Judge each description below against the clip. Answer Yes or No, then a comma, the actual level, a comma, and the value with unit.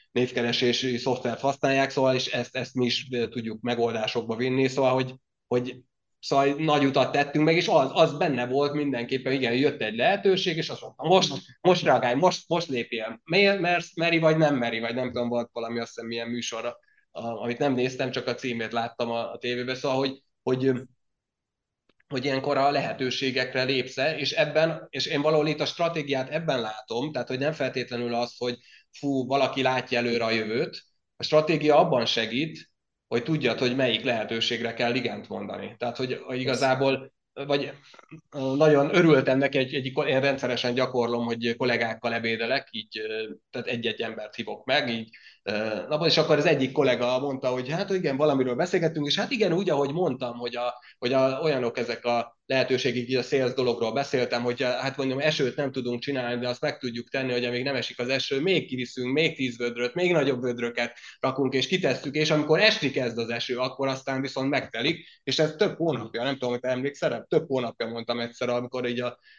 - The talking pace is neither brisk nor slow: No, fast, 185 wpm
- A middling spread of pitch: Yes, average, 3.1 semitones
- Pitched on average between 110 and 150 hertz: Yes, low, 130 Hz